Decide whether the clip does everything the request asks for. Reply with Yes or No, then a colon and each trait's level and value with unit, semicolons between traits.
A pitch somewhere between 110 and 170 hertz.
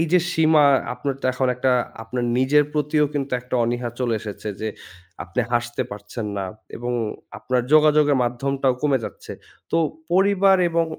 Yes: low, 135 Hz